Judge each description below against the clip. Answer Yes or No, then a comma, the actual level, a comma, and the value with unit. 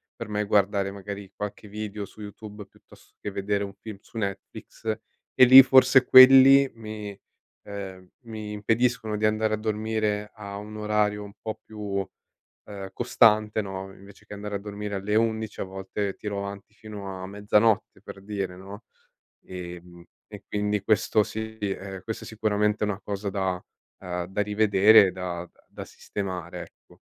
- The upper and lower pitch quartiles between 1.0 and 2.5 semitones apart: Yes, narrow, 1.7 semitones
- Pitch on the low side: Yes, low, 105 Hz